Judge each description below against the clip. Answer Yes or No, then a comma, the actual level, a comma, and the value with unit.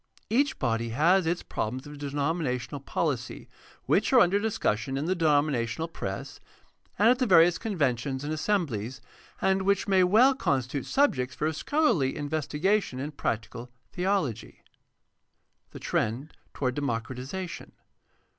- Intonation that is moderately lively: No, wide, 6.6 semitones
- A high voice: No, medium, 150 Hz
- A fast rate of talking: No, slow, 135 wpm